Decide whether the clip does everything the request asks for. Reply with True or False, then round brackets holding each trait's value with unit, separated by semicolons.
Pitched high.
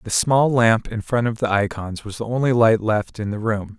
False (110 Hz)